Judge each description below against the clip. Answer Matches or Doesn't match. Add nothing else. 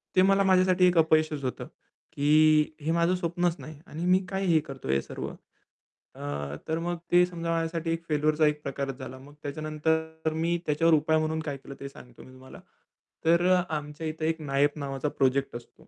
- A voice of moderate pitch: Matches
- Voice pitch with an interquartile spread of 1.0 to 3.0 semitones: Matches